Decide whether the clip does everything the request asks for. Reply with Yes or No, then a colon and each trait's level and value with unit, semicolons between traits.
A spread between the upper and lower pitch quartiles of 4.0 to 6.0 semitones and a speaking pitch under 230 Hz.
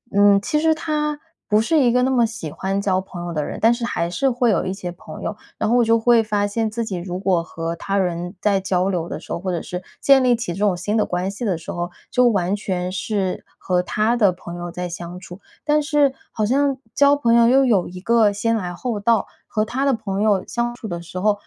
Yes: average, 4.7 semitones; high, 205 Hz